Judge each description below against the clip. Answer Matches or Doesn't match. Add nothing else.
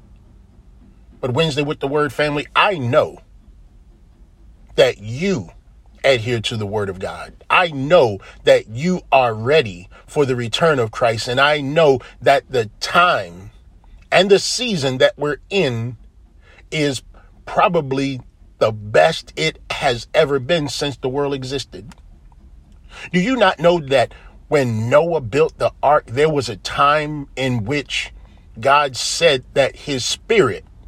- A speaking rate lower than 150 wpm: Matches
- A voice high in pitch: Doesn't match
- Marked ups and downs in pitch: Matches